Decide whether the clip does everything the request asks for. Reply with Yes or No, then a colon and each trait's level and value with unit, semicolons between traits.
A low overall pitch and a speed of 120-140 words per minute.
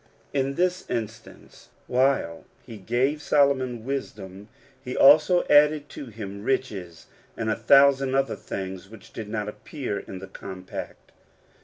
Yes: low, 125 Hz; slow, 135 wpm